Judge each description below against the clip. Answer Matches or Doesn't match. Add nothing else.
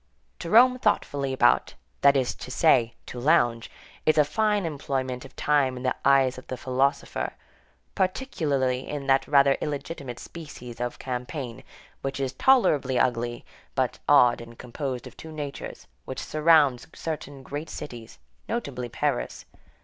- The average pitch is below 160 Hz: Matches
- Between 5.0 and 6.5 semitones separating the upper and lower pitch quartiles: Doesn't match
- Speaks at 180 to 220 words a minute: Doesn't match